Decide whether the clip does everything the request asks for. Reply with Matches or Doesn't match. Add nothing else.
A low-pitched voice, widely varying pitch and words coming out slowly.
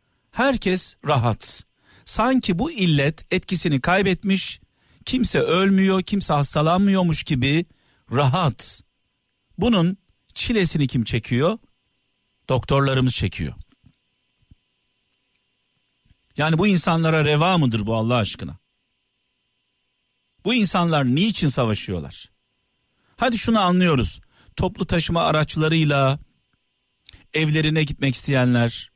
Doesn't match